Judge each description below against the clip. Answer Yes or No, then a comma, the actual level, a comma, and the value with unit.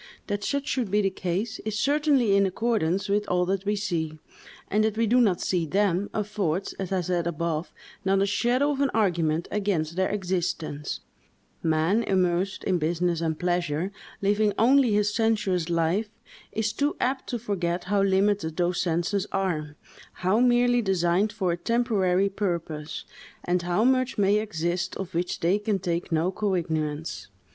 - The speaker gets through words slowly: No, average, 165 wpm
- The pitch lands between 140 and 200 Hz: Yes, high, 190 Hz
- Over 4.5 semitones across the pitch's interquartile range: No, average, 3.4 semitones